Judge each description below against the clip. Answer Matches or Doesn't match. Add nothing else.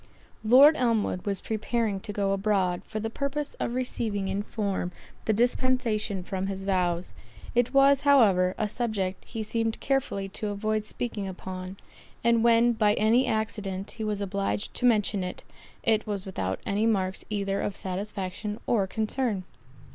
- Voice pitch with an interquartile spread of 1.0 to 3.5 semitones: Matches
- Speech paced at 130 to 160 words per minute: Matches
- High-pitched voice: Matches